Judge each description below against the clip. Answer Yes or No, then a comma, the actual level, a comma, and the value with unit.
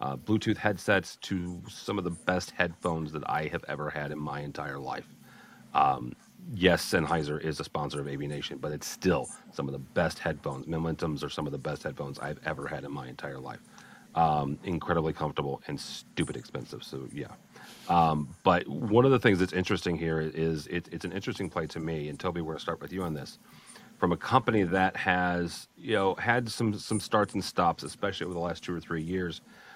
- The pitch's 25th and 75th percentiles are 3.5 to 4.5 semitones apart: Yes, average, 3.9 semitones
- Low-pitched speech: Yes, very low, 85 Hz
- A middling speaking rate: No, fast, 210 wpm